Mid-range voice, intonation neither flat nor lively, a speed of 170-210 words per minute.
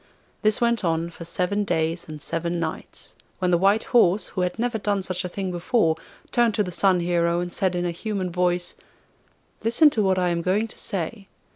Yes: medium, 180 Hz; average, 3.3 semitones; average, 200 wpm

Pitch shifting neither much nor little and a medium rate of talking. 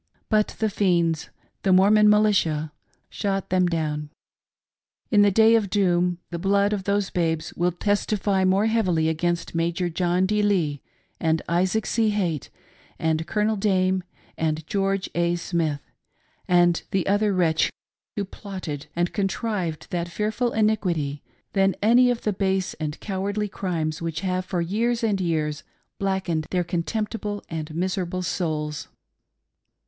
Yes: average, 3.5 semitones; average, 145 wpm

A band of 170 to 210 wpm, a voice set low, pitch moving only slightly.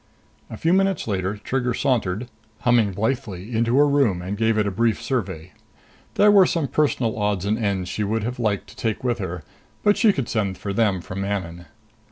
No: average, 200 wpm; low, 110 Hz; average, 4.2 semitones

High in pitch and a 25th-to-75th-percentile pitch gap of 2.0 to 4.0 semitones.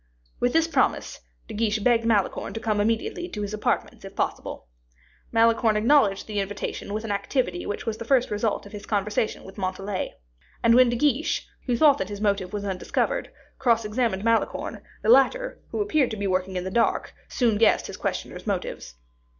Yes: high, 220 Hz; average, 2.9 semitones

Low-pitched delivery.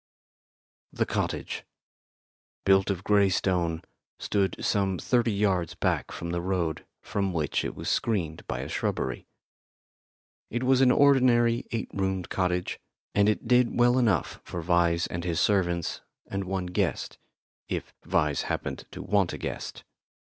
Yes: very low, 95 Hz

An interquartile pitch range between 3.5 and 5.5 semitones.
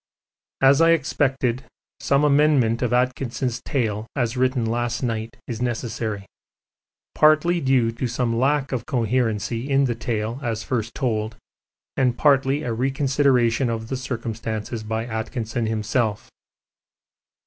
No: average, 2.9 semitones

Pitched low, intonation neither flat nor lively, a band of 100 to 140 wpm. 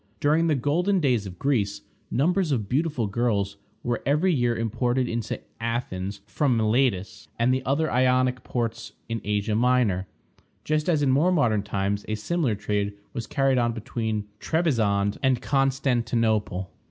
No: low, 120 Hz; average, 4.5 semitones; average, 150 wpm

